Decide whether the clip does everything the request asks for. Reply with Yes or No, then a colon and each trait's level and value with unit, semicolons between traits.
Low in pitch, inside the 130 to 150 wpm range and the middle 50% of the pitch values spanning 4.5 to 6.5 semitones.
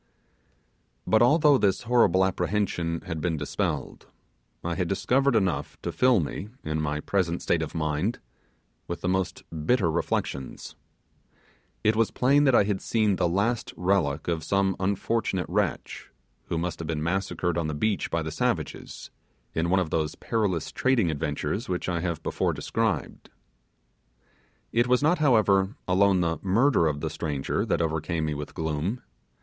No: very low, 90 Hz; average, 160 wpm; average, 4.9 semitones